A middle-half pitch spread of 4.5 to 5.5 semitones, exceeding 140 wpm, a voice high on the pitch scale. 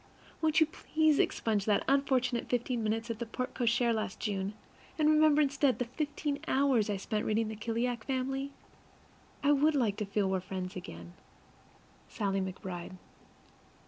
Yes: average, 5.0 semitones; average, 160 wpm; high, 235 Hz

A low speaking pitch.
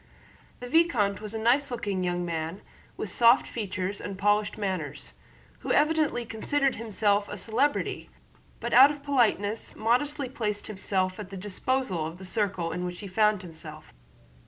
No: high, 210 Hz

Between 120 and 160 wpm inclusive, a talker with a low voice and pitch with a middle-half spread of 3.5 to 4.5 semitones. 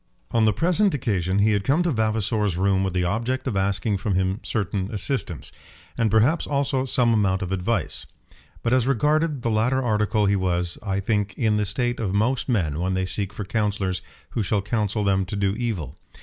No: average, 200 wpm; low, 105 Hz; average, 3.8 semitones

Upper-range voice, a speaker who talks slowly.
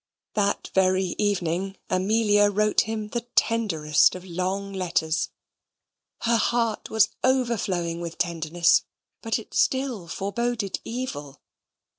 Yes: high, 200 Hz; slow, 110 wpm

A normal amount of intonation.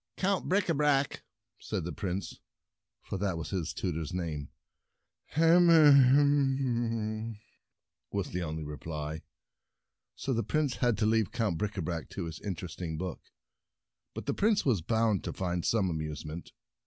No: wide, 7.9 semitones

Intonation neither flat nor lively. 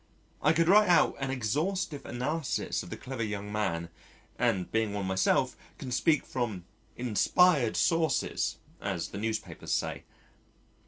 No: wide, 6.9 semitones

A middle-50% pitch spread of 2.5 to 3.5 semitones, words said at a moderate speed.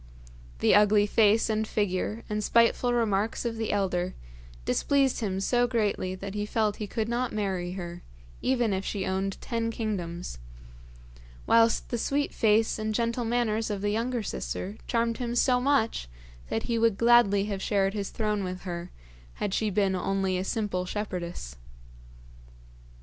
Yes: average, 3.1 semitones; average, 160 wpm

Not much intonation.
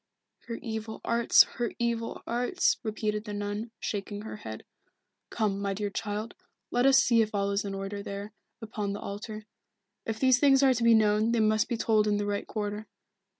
Yes: narrow, 2.2 semitones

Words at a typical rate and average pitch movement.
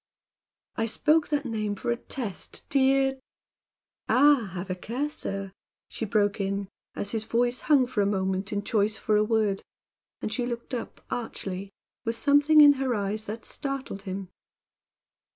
Yes: average, 165 wpm; average, 4.8 semitones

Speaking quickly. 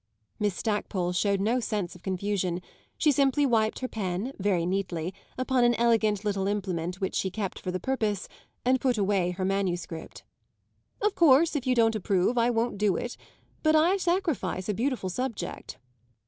No: average, 170 wpm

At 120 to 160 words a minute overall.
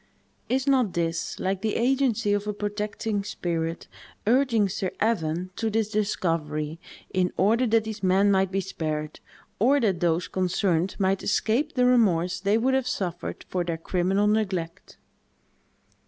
Yes: average, 150 wpm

